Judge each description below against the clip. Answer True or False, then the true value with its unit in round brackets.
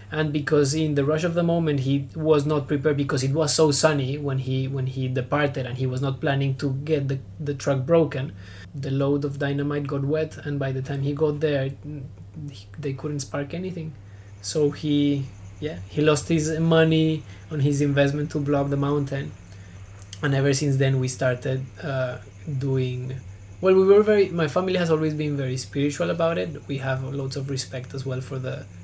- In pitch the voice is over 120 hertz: True (140 Hz)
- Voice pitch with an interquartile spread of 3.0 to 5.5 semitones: False (2.4 semitones)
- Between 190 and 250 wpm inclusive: True (200 wpm)